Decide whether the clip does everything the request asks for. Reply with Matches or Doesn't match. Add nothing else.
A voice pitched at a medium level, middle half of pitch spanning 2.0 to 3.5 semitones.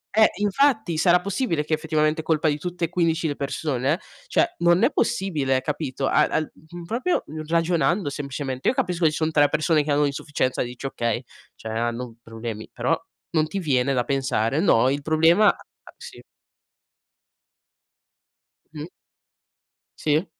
Doesn't match